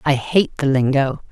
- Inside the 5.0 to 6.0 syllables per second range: No, 4.6 syllables/s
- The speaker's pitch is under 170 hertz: Yes, medium, 140 Hz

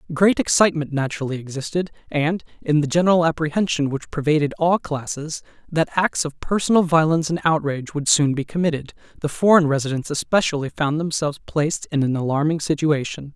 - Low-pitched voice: No, medium, 155 Hz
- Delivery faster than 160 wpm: No, average, 155 wpm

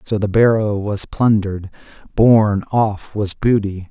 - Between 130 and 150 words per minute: Yes, average, 140 wpm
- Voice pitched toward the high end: No, low, 105 Hz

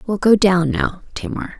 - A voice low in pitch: No, high, 195 Hz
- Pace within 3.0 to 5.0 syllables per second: Yes, 4.5 syllables/s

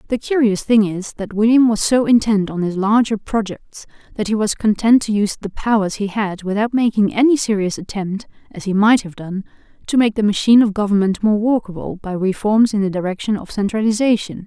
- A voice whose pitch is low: No, high, 210 Hz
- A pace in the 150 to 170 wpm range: No, average, 200 wpm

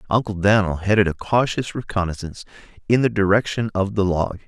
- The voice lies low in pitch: Yes, low, 100 Hz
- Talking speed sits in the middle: Yes, average, 160 wpm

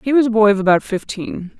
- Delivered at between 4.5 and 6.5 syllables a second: Yes, 6.2 syllables/s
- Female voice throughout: Yes, female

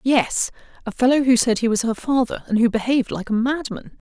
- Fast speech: Yes, fast, 220 wpm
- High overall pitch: Yes, high, 240 Hz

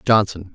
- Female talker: No, male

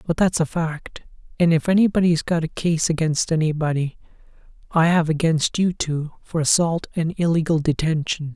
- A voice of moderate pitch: Yes, medium, 160 Hz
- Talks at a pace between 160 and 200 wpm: No, average, 150 wpm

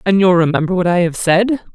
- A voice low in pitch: No, medium, 185 Hz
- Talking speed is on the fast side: Yes, fast, 240 wpm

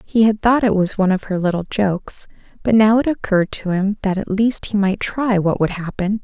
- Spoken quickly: Yes, fast, 240 wpm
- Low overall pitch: No, high, 200 Hz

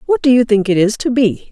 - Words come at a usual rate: No, fast, 315 wpm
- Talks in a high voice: Yes, high, 235 Hz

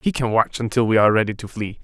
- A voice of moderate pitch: No, low, 110 Hz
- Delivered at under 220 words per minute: No, fast, 295 wpm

